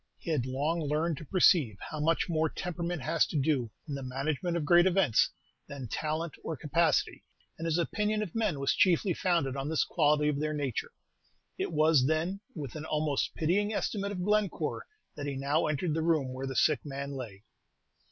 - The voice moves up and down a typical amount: Yes, average, 3.5 semitones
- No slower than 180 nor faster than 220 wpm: Yes, average, 190 wpm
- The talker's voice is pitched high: No, medium, 155 Hz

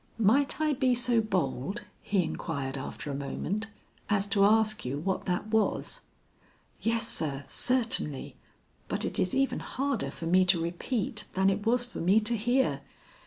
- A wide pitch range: Yes, wide, 5.7 semitones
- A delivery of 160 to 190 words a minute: Yes, average, 165 wpm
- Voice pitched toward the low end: No, high, 210 Hz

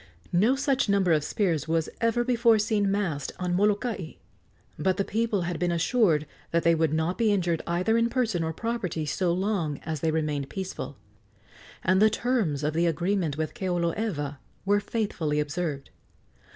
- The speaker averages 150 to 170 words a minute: Yes, average, 165 wpm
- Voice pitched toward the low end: No, medium, 180 Hz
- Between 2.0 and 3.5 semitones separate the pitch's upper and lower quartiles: No, average, 5.0 semitones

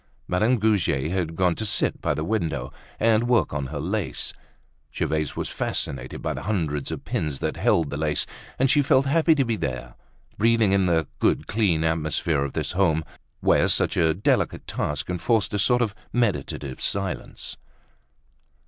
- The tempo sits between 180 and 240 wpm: No, average, 170 wpm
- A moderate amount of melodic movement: No, wide, 6.2 semitones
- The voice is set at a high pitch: No, very low, 90 Hz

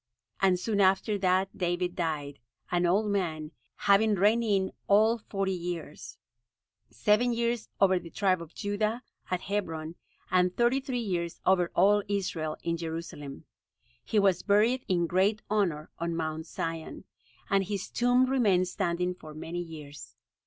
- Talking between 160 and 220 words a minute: No, average, 145 wpm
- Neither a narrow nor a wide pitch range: Yes, average, 3.6 semitones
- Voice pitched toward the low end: No, medium, 185 Hz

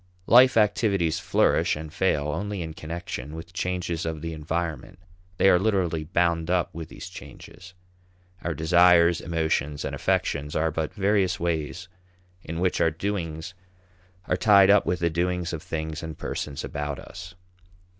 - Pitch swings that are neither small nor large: No, narrow, 2.3 semitones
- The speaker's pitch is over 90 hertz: No, very low, 85 Hz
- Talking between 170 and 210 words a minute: No, average, 155 wpm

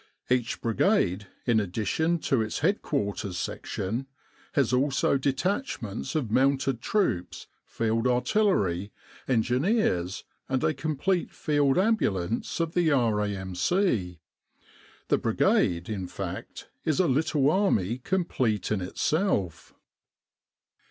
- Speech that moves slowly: Yes, slow, 105 wpm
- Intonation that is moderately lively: No, wide, 7.4 semitones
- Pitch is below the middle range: Yes, low, 125 Hz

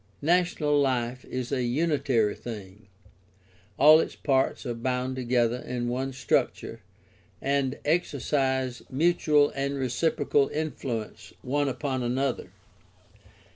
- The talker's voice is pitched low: Yes, low, 130 Hz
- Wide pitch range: No, average, 2.8 semitones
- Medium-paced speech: No, slow, 105 wpm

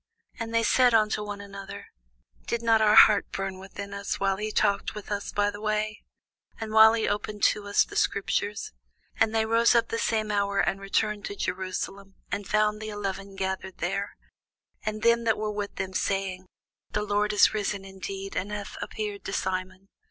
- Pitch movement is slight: Yes, narrow, 1.6 semitones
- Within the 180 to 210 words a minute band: Yes, average, 190 wpm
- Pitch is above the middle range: Yes, high, 205 Hz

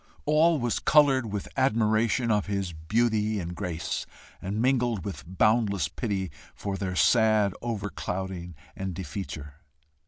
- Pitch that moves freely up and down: No, average, 3.7 semitones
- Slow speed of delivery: Yes, slow, 125 wpm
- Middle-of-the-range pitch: No, low, 105 Hz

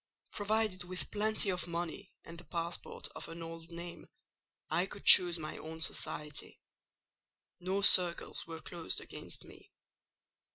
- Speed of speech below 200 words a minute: Yes, slow, 135 wpm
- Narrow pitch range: Yes, narrow, 2.1 semitones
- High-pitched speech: No, medium, 175 Hz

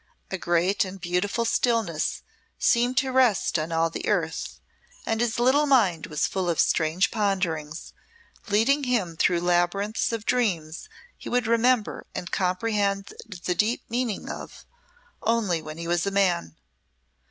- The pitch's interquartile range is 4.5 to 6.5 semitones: Yes, average, 5.2 semitones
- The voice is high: Yes, high, 195 Hz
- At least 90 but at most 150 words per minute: Yes, average, 145 wpm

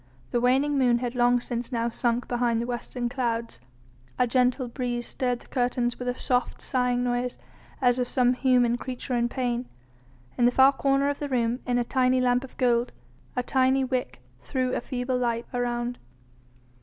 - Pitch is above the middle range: Yes, high, 245 Hz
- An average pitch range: No, narrow, 1.1 semitones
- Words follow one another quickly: No, average, 180 wpm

